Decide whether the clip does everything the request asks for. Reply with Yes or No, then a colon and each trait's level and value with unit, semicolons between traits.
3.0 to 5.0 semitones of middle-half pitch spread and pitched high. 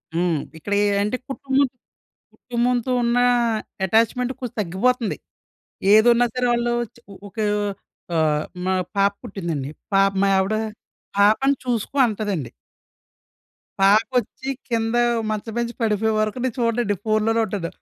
Yes: average, 3.4 semitones; high, 220 Hz